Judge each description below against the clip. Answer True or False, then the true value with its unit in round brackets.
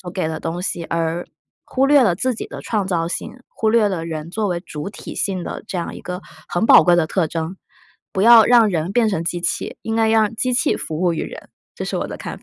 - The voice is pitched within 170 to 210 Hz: True (185 Hz)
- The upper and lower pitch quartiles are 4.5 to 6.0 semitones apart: True (4.8 semitones)